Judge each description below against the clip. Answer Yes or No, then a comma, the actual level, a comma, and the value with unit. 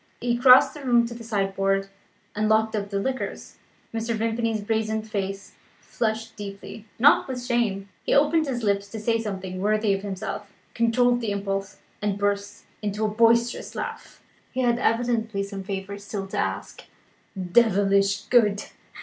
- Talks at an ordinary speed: Yes, average, 160 wpm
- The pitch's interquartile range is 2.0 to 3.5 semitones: Yes, average, 2.8 semitones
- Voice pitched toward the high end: Yes, high, 215 Hz